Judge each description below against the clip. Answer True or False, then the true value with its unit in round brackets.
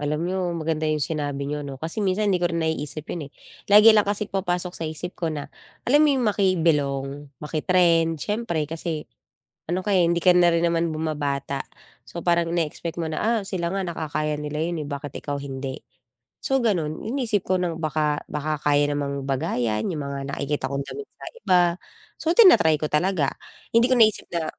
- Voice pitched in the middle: True (165 Hz)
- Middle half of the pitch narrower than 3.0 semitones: False (3.7 semitones)